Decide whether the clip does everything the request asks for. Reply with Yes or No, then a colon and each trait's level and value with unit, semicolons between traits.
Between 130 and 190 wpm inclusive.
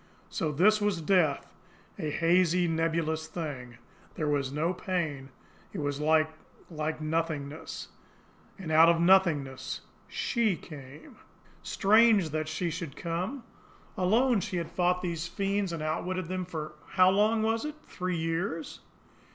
Yes: average, 140 wpm